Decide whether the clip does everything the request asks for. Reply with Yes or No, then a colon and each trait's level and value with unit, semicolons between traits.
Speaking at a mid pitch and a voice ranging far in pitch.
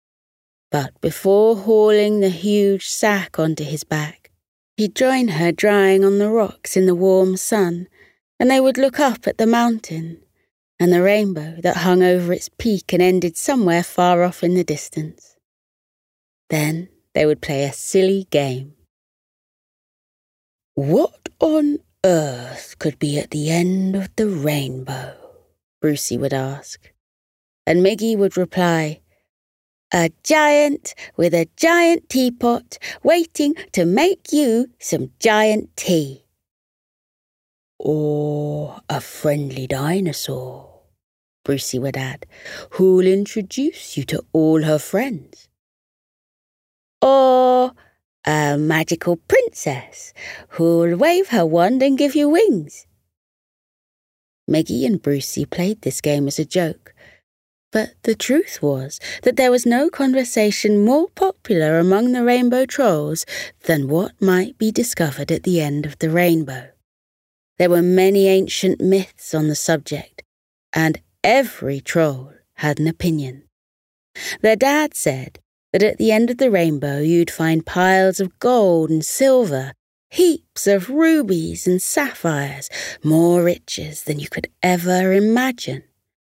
Yes: medium, 180 Hz; wide, 6.4 semitones